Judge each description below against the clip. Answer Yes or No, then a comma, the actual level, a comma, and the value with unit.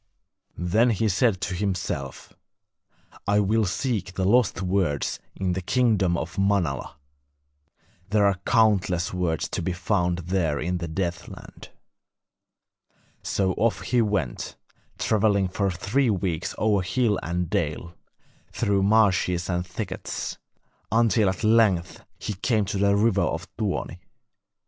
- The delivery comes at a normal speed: No, slow, 130 wpm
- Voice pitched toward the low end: Yes, very low, 95 Hz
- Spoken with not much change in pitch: No, average, 3.2 semitones